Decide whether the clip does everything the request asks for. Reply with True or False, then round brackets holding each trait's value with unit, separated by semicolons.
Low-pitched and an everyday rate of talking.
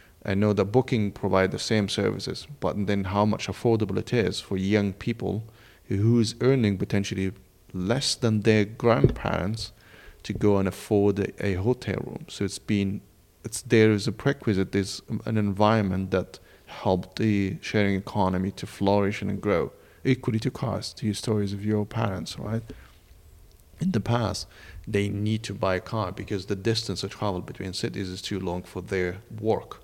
True (100 Hz; 170 wpm)